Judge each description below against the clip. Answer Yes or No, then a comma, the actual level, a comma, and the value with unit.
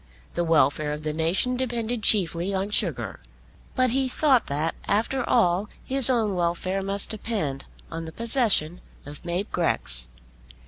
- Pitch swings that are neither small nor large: No, wide, 6.1 semitones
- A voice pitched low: No, high, 190 Hz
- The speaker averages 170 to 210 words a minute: No, average, 145 wpm